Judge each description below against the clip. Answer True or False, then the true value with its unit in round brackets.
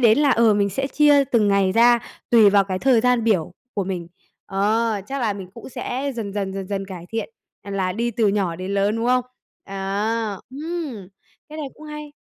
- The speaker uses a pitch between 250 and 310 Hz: False (220 Hz)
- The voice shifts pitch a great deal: False (4.1 semitones)